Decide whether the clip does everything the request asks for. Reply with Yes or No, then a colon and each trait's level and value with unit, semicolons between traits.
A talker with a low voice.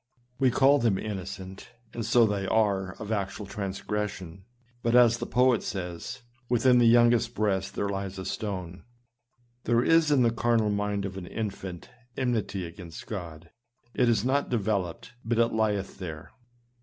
Yes: low, 105 Hz